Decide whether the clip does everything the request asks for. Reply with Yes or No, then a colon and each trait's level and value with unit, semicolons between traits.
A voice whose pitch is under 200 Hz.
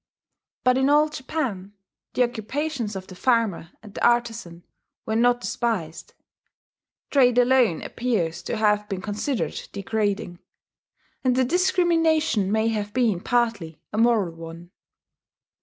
No: high, 225 Hz